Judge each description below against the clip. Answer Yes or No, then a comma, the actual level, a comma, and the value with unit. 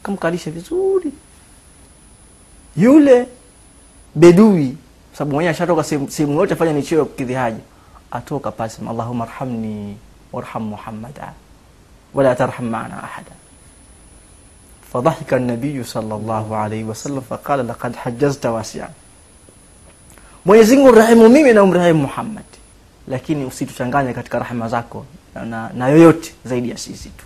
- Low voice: Yes, low, 130 Hz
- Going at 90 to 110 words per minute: Yes, average, 105 wpm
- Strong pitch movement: Yes, wide, 6.7 semitones